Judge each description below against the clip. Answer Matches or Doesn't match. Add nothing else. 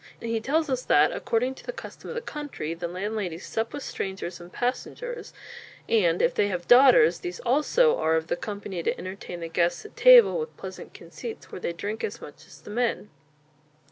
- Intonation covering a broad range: Matches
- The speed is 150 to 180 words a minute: Doesn't match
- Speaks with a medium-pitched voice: Doesn't match